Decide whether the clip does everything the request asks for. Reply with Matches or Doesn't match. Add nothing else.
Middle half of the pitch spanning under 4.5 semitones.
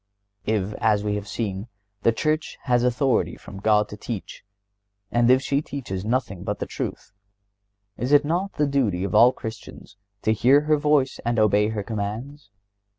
Doesn't match